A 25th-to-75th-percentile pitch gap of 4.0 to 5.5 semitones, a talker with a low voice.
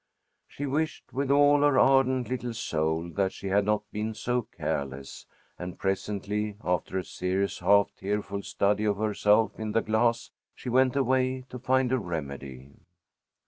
Yes: average, 4.9 semitones; low, 105 Hz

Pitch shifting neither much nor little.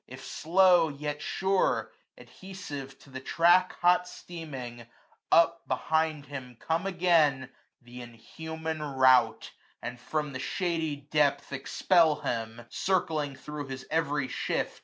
Yes: average, 4.0 semitones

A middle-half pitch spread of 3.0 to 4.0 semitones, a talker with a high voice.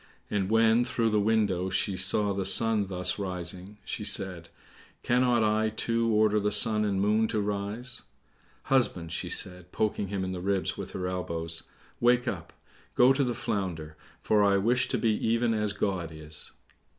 No: average, 3.3 semitones; low, 100 Hz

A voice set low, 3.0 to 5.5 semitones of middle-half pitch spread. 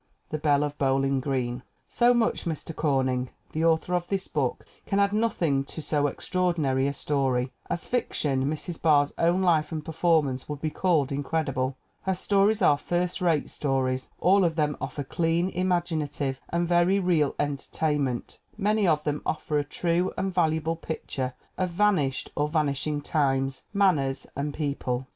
No: medium, 155 Hz; average, 4.0 semitones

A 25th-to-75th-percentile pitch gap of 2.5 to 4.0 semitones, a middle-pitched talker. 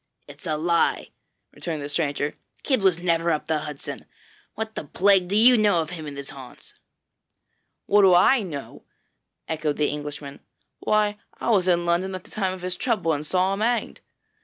No: average, 4.6 semitones; medium, 175 Hz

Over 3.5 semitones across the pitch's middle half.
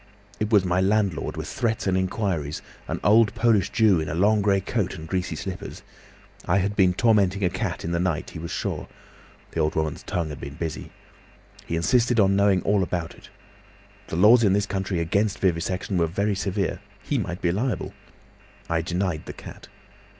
No: average, 3.2 semitones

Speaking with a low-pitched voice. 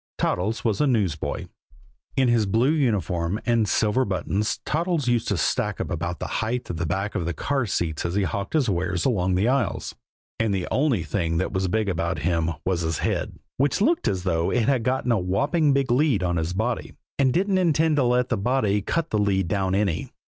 Yes: low, 105 Hz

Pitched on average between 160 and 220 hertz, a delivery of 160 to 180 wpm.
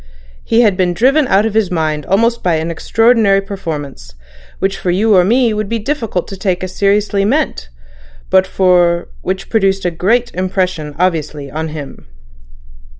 Yes: high, 190 Hz; average, 165 wpm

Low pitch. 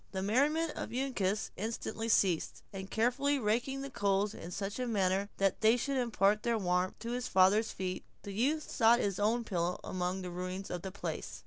No: high, 210 Hz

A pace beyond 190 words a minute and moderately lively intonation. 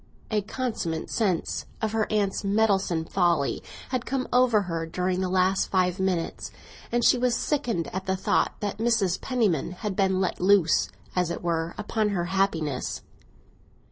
No: average, 160 wpm; average, 3.7 semitones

